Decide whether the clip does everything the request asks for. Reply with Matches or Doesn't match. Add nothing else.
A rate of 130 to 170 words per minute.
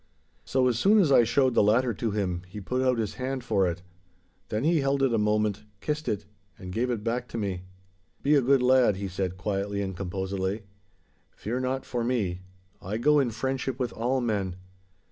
Doesn't match